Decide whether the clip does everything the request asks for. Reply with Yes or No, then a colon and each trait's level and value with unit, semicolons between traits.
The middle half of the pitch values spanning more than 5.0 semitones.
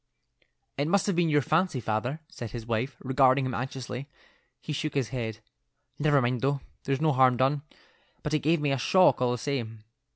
No: average, 3.3 semitones